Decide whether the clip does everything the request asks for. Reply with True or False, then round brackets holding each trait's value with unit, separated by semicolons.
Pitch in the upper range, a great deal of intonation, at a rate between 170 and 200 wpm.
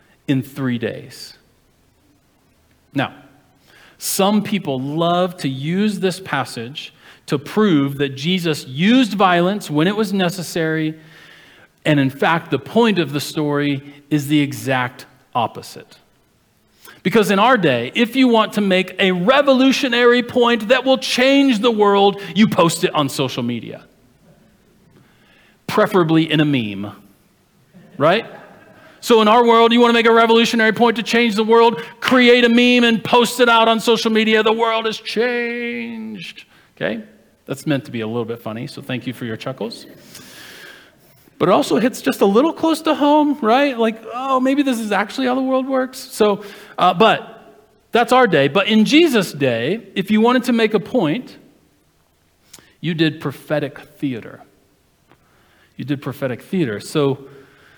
False (205 Hz; 7.9 semitones; 160 wpm)